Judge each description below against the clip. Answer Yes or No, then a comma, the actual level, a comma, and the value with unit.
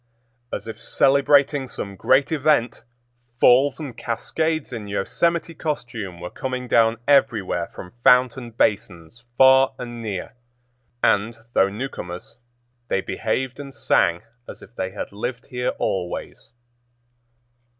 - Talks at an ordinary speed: No, slow, 120 wpm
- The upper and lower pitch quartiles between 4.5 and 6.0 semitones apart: Yes, average, 4.8 semitones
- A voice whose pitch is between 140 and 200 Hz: No, low, 120 Hz